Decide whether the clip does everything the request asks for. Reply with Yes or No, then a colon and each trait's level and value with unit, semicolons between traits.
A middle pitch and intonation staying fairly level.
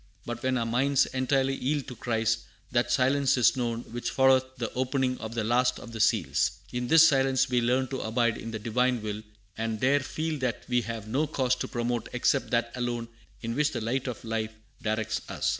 No: low, 125 Hz; narrow, 2.3 semitones